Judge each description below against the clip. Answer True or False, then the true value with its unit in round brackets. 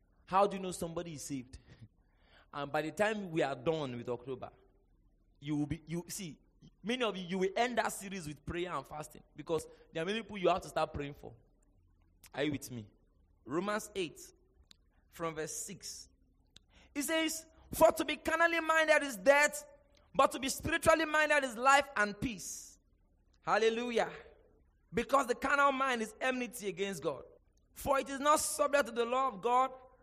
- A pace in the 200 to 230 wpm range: False (180 wpm)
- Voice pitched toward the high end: True (195 Hz)